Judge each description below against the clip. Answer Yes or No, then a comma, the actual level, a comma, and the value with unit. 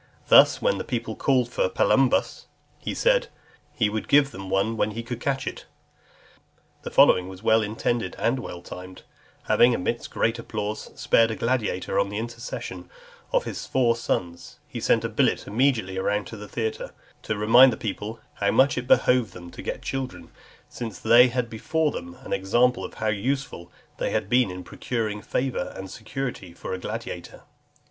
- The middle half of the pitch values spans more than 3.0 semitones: Yes, average, 3.7 semitones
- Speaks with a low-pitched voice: Yes, low, 115 Hz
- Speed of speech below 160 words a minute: No, average, 175 wpm